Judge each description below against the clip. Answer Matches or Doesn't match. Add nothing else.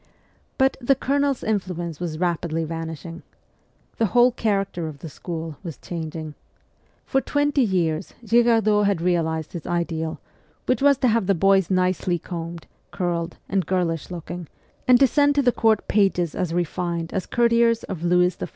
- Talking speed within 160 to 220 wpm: Matches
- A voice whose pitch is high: Doesn't match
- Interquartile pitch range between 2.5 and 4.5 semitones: Doesn't match